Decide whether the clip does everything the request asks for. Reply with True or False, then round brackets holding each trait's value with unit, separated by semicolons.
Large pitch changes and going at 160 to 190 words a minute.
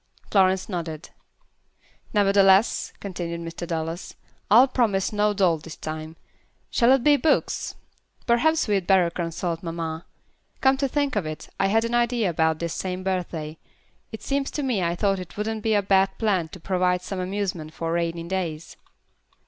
False (4.1 semitones; 165 wpm)